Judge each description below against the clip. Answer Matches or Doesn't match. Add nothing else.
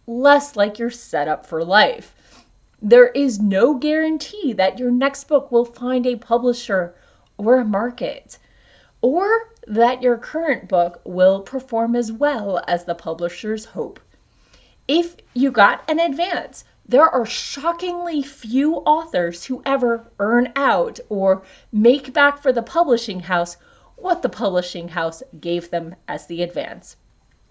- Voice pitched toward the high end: Matches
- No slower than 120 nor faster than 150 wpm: Matches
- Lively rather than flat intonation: Matches